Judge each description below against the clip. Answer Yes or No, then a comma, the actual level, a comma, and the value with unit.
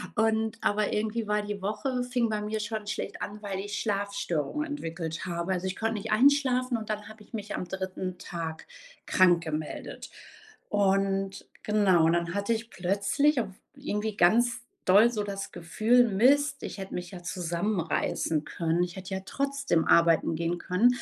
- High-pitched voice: Yes, high, 205 Hz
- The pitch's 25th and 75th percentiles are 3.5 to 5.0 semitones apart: Yes, average, 3.8 semitones